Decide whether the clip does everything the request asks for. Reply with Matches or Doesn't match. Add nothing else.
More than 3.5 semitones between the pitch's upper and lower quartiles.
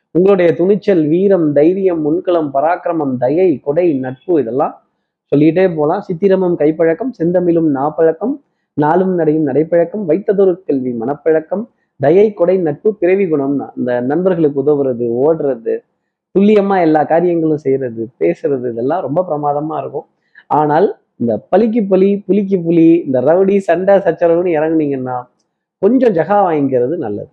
Matches